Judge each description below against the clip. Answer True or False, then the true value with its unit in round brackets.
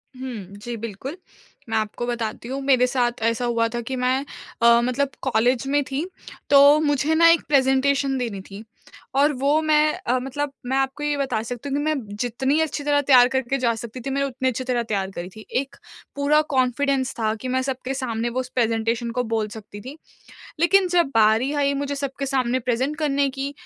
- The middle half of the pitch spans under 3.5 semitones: True (3.0 semitones)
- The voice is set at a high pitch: True (260 Hz)